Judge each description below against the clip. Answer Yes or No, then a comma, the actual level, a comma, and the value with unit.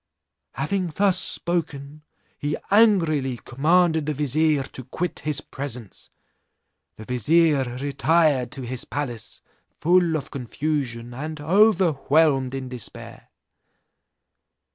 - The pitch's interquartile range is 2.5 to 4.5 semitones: Yes, average, 4.0 semitones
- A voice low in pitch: No, medium, 145 Hz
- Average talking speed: No, slow, 100 wpm